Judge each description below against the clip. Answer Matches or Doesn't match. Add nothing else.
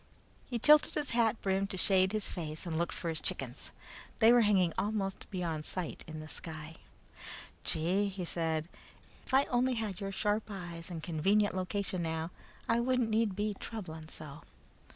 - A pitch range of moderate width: Matches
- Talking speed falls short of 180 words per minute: Matches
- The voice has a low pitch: Doesn't match